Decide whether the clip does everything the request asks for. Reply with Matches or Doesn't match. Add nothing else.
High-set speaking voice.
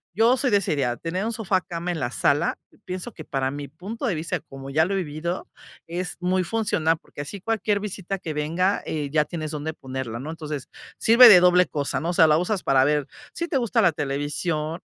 Doesn't match